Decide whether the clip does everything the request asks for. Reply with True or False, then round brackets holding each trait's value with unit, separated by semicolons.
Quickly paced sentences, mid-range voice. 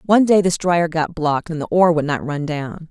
True (270 wpm; 165 Hz)